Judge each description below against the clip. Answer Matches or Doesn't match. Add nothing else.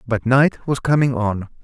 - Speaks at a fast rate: Doesn't match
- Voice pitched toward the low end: Matches